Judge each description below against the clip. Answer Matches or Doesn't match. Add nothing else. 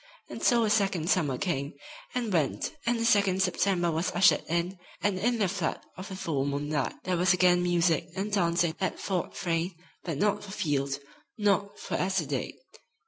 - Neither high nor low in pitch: Matches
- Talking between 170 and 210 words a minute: Matches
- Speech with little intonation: Doesn't match